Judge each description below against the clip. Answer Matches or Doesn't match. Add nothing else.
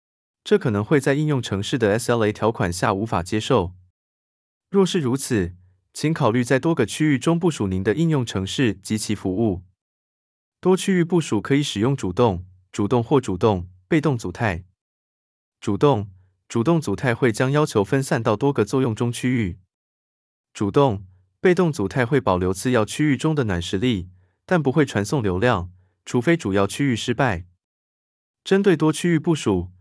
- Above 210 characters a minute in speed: Matches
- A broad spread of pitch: Matches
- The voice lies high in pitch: Doesn't match